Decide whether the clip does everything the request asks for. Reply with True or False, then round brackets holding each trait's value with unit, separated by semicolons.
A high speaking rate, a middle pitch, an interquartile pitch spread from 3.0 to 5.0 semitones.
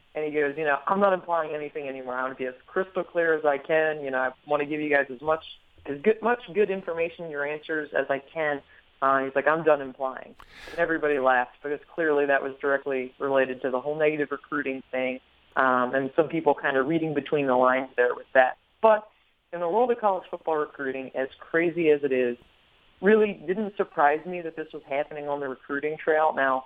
True (225 wpm; 145 Hz; 3.4 semitones)